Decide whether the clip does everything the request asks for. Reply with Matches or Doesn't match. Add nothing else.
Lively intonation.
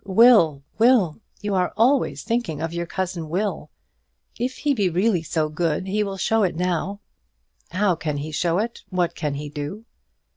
Doesn't match